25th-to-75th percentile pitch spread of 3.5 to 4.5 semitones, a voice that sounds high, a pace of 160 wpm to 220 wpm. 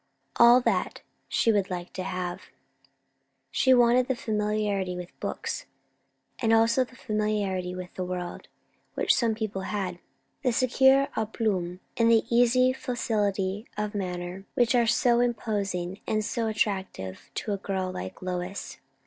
No: average, 4.1 semitones; high, 210 Hz; average, 145 wpm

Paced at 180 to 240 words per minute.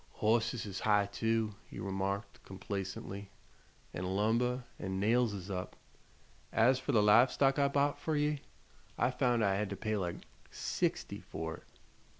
No: average, 155 wpm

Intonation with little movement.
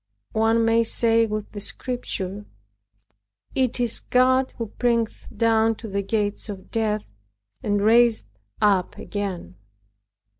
Yes: narrow, 2.1 semitones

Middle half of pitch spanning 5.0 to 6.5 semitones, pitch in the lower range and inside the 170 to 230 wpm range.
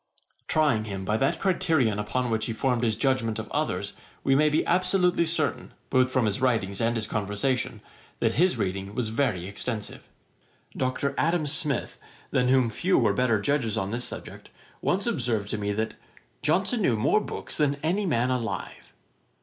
Yes: wide, 5.5 semitones; low, 125 Hz; average, 175 wpm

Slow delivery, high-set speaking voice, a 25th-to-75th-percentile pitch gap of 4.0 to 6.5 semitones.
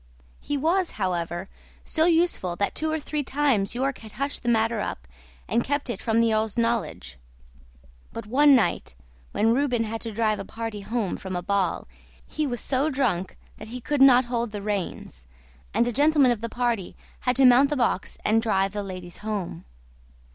No: average, 190 wpm; high, 230 Hz; average, 4.8 semitones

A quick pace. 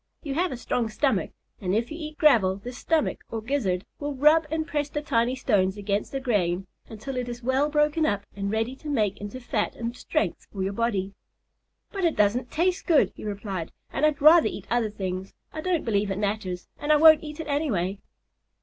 Yes: fast, 210 wpm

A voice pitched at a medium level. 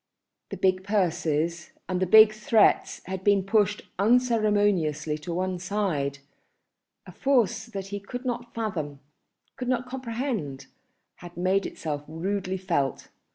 No: high, 195 Hz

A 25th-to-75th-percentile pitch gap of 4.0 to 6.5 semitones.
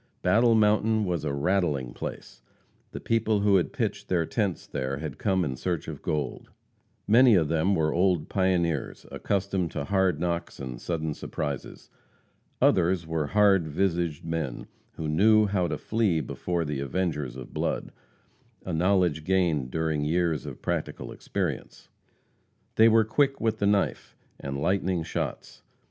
Yes: average, 4.3 semitones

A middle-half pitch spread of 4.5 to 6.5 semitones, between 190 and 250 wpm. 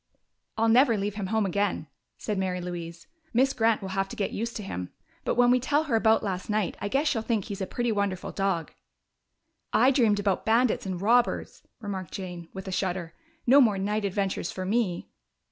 No: average, 3.3 semitones; average, 200 wpm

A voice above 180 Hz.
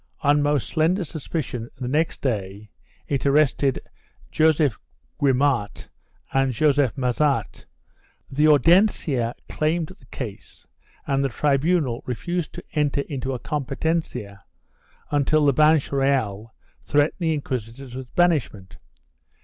No: medium, 140 Hz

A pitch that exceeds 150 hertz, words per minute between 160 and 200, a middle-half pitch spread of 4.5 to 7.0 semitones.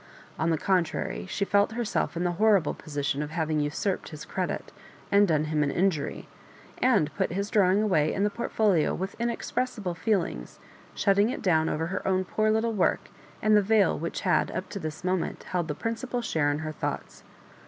Yes: medium, 185 Hz; average, 190 wpm; average, 4.8 semitones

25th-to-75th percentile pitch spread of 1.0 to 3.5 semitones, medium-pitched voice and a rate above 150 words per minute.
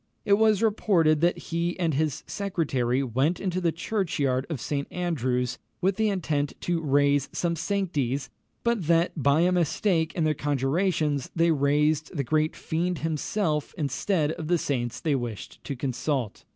No: average, 3.9 semitones; medium, 155 Hz; average, 160 wpm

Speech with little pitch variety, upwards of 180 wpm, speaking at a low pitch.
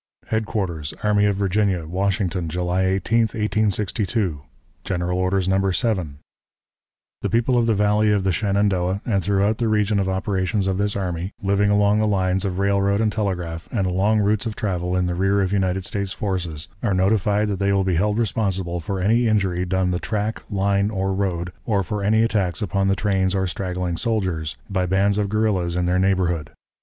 Yes: narrow, 2.3 semitones; average, 190 wpm; very low, 95 Hz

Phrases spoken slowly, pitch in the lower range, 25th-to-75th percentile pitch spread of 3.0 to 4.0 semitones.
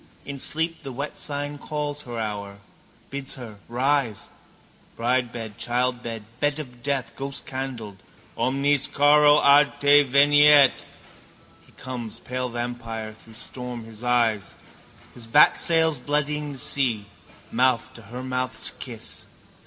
Yes: slow, 125 wpm; low, 130 Hz; average, 3.4 semitones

